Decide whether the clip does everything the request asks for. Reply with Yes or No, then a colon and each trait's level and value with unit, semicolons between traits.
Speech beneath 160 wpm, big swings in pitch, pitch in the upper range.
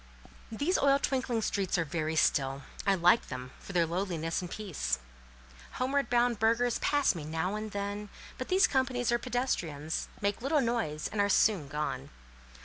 No: average, 165 wpm; wide, 6.9 semitones; high, 205 Hz